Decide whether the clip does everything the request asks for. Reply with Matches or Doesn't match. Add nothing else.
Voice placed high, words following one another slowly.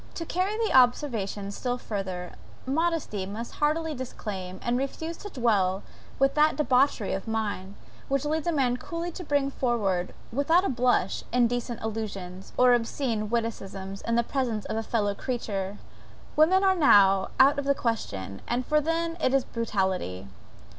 Doesn't match